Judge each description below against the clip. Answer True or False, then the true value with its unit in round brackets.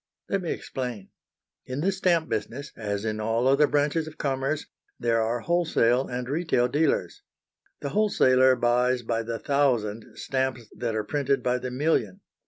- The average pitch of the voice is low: True (130 Hz)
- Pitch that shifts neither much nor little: True (3.9 semitones)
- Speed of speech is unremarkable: True (160 wpm)